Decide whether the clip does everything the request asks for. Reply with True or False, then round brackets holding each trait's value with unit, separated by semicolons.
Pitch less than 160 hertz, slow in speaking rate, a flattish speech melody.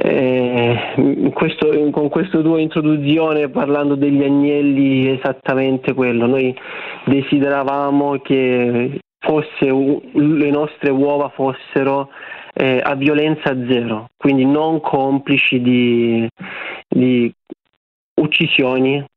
True (140 Hz; 90 wpm; 2.2 semitones)